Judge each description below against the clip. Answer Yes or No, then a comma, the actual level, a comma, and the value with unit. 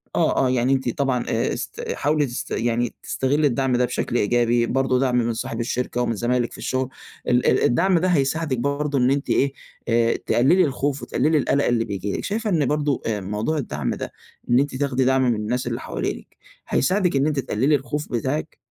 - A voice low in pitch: Yes, low, 130 Hz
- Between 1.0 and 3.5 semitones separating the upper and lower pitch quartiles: Yes, average, 3.1 semitones